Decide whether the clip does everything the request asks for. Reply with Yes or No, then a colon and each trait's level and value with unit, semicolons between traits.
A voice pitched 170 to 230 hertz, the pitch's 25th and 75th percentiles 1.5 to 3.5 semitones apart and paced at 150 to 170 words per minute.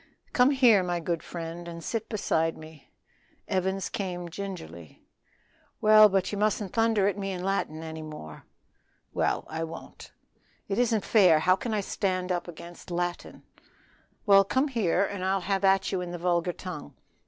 Yes: medium, 185 Hz; average, 2.9 semitones; average, 165 wpm